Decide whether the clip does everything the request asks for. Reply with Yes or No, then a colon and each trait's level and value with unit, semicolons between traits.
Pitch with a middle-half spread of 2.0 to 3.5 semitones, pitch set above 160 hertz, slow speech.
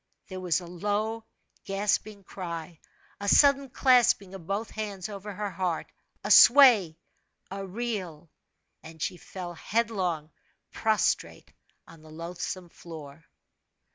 No: average, 4.0 semitones; high, 190 Hz; slow, 120 wpm